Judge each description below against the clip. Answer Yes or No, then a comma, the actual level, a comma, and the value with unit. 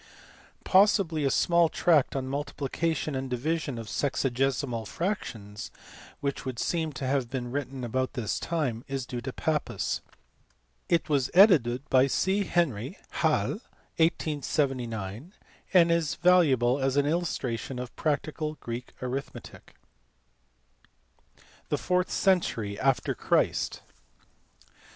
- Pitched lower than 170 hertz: Yes, medium, 140 Hz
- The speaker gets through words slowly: Yes, slow, 115 wpm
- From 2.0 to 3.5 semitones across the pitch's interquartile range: No, average, 4.7 semitones